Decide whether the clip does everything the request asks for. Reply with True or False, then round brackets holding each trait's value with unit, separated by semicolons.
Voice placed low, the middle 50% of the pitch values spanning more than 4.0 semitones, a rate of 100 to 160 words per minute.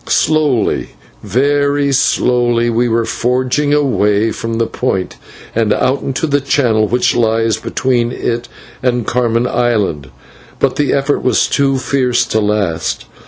False (120 Hz; 3.2 semitones; 135 wpm)